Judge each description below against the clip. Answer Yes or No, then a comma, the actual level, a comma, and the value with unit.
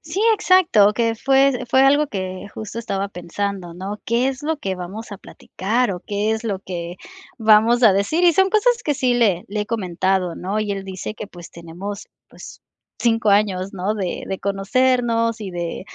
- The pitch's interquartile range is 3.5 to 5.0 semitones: Yes, average, 4.2 semitones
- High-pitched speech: Yes, high, 210 Hz